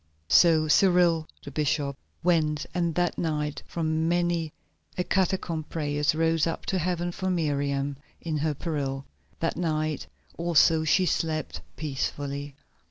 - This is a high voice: No, medium, 160 Hz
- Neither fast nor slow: No, slow, 130 wpm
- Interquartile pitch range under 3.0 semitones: Yes, narrow, 2.6 semitones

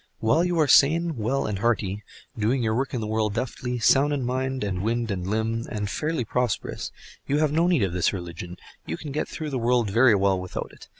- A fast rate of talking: Yes, fast, 220 wpm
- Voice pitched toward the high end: No, low, 115 Hz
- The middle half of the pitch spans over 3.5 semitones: Yes, average, 4.6 semitones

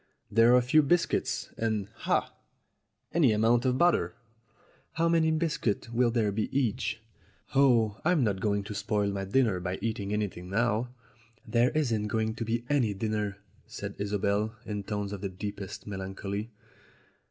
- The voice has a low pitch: Yes, low, 110 Hz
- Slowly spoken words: No, average, 160 wpm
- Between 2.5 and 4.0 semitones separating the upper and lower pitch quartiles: Yes, average, 3.2 semitones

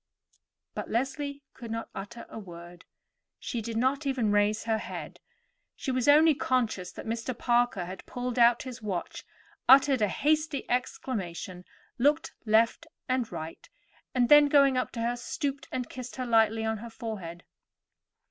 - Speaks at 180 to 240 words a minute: No, average, 155 wpm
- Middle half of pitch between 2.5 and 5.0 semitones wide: Yes, average, 3.5 semitones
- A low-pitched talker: No, high, 240 Hz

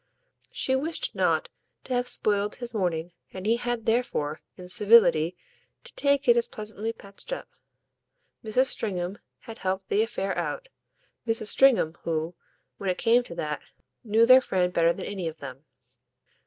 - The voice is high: Yes, high, 210 Hz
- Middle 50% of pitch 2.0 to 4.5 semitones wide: No, average, 5.2 semitones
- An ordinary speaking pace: Yes, average, 160 wpm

